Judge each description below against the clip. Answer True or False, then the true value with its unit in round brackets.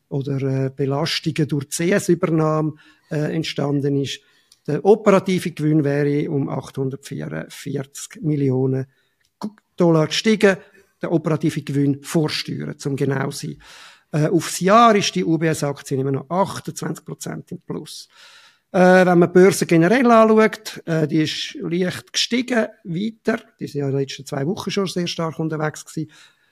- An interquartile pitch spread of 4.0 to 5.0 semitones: True (4.6 semitones)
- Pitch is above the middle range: False (160 Hz)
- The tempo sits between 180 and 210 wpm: False (140 wpm)